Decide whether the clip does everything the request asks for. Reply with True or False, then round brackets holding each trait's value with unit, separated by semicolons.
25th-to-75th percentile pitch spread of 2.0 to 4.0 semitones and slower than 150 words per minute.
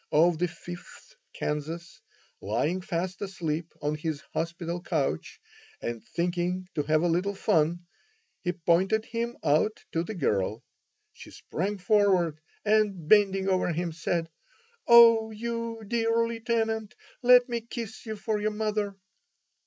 False (4.7 semitones; 135 wpm)